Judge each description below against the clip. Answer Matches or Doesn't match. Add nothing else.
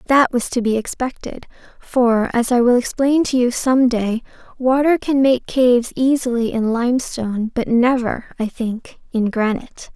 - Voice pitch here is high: Matches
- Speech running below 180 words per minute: Matches